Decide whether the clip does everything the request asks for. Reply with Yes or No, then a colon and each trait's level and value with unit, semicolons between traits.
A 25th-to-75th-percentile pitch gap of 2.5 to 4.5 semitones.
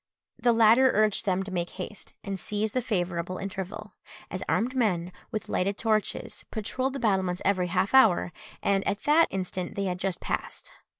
Yes: average, 3.0 semitones